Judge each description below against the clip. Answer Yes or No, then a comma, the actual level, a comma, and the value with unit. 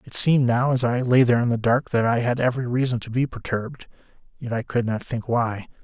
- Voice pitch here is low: Yes, low, 120 Hz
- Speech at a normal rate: No, fast, 245 wpm